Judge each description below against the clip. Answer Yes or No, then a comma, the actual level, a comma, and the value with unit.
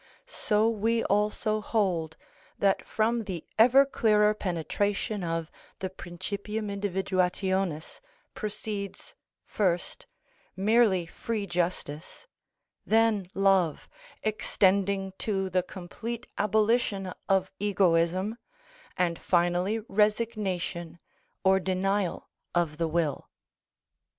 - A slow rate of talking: Yes, slow, 90 wpm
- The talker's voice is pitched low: No, high, 195 Hz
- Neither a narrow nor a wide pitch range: Yes, average, 3.0 semitones